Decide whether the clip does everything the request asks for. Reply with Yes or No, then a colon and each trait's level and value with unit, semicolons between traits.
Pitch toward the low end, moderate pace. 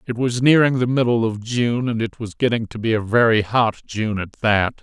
No: low, 115 Hz; fast, 235 wpm